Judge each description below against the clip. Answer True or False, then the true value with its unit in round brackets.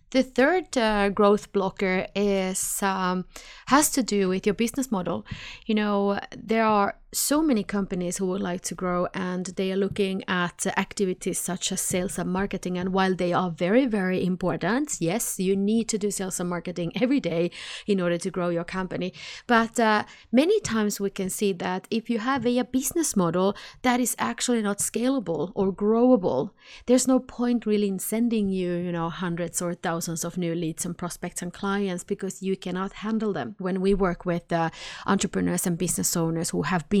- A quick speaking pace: False (190 wpm)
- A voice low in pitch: False (190 Hz)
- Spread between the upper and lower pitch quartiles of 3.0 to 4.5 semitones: True (3.5 semitones)